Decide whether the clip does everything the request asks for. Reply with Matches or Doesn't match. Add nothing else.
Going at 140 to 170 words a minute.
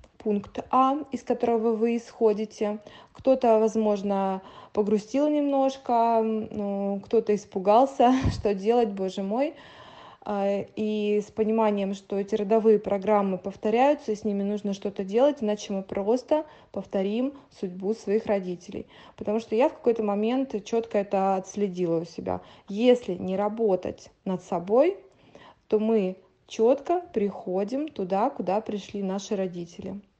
Doesn't match